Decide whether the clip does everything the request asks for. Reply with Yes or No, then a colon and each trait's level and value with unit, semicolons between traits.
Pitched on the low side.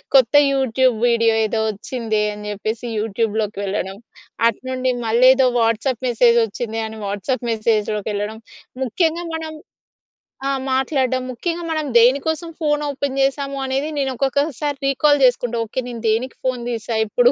No: very high, 250 Hz